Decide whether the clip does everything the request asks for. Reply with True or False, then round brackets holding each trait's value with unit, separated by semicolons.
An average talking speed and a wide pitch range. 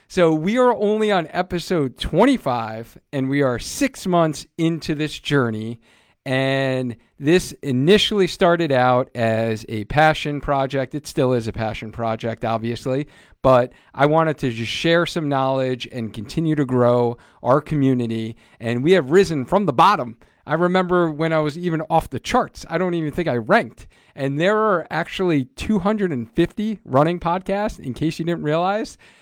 True (160 wpm; 5.7 semitones)